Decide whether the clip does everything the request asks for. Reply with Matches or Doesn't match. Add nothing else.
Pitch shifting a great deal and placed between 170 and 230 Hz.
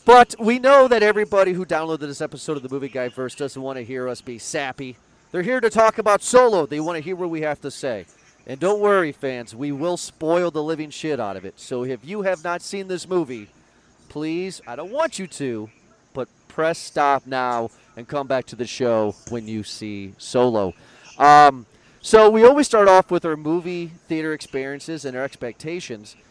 Doesn't match